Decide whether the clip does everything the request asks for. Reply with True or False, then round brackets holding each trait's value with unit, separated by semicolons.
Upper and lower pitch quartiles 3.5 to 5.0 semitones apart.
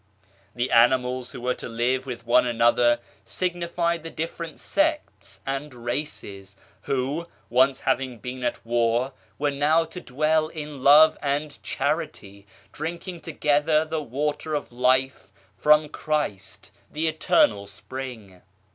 True (4.3 semitones)